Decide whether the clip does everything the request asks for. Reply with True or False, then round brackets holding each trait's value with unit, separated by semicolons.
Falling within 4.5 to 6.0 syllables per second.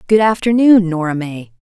True (5.0 syllables/s)